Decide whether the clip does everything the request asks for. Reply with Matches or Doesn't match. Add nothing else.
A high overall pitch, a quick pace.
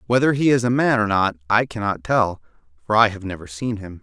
Doesn't match